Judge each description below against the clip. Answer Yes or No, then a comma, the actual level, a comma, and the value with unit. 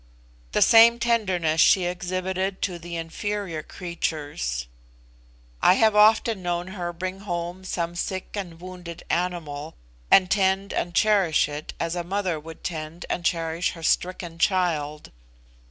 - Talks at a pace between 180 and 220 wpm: No, average, 140 wpm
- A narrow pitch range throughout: Yes, narrow, 2.3 semitones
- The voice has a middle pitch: Yes, medium, 175 Hz